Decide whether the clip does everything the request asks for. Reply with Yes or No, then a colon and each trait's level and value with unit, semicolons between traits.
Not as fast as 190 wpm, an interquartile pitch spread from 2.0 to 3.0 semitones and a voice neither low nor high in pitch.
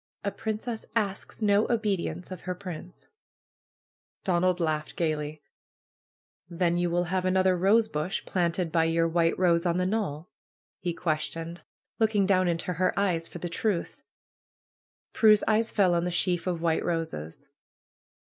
Yes: average, 150 wpm; average, 2.7 semitones; medium, 180 Hz